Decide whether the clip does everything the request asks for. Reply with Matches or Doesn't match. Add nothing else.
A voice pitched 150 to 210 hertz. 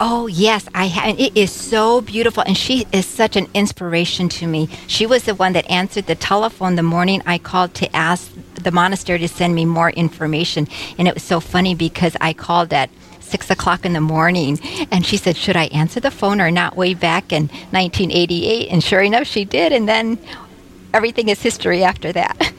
Matches